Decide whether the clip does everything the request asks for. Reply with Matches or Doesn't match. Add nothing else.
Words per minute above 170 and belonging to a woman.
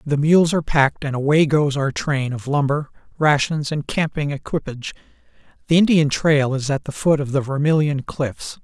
Doesn't match